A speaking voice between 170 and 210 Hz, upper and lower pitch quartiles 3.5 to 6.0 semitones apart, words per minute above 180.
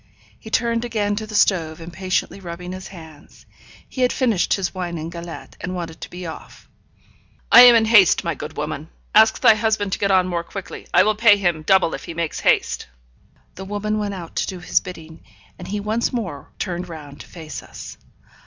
Yes: medium, 185 Hz; average, 3.8 semitones; fast, 205 wpm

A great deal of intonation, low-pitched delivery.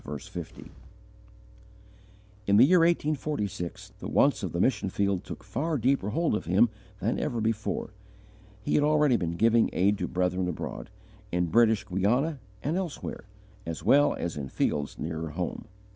Yes: wide, 8.0 semitones; low, 110 Hz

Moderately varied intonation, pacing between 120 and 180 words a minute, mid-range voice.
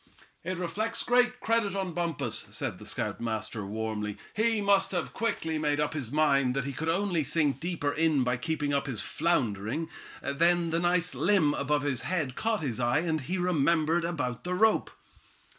Yes: average, 4.6 semitones; average, 175 wpm; medium, 160 Hz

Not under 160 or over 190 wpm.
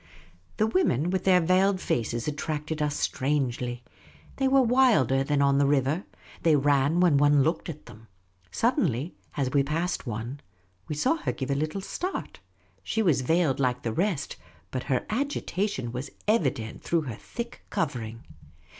Yes: average, 165 wpm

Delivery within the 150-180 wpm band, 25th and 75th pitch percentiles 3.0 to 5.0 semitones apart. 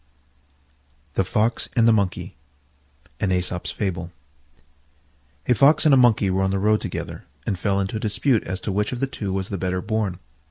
Yes: average, 170 wpm; average, 3.6 semitones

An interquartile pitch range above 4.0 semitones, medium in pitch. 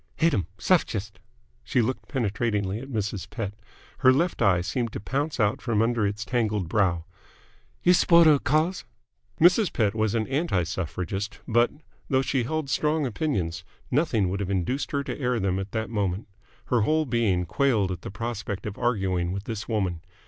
No: wide, 5.4 semitones; low, 110 Hz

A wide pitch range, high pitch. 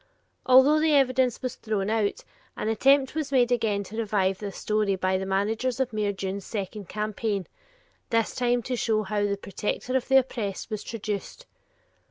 No: average, 3.9 semitones; high, 220 Hz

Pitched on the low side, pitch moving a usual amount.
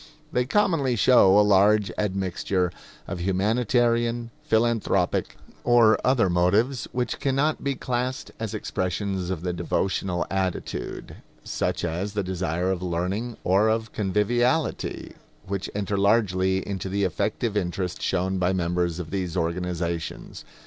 Yes: low, 100 Hz; average, 4.3 semitones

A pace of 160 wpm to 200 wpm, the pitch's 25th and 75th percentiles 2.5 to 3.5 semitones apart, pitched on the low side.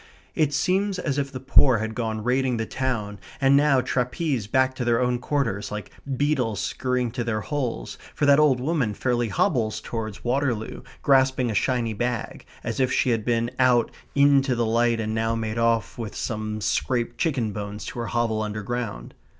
Yes: average, 180 wpm; average, 3.1 semitones; low, 120 Hz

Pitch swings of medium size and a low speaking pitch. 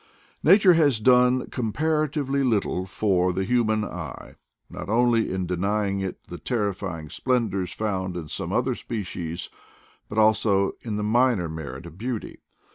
Yes: average, 4.9 semitones; low, 105 Hz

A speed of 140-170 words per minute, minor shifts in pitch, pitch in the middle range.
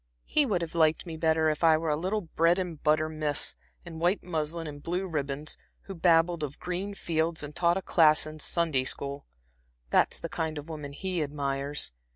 No: average, 195 wpm; narrow, 2.3 semitones; medium, 160 Hz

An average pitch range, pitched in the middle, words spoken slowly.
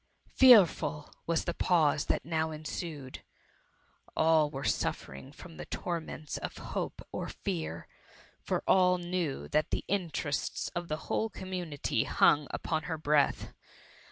Yes: average, 3.0 semitones; medium, 160 Hz; slow, 130 wpm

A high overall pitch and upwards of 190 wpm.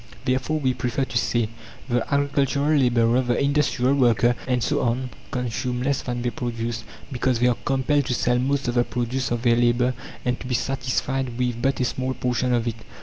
No: low, 125 Hz; average, 200 wpm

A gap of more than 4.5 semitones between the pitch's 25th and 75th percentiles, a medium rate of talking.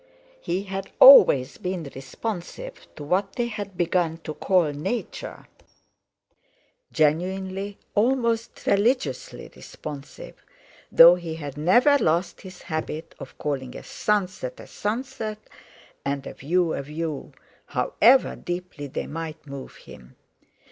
No: wide, 5.4 semitones; slow, 120 wpm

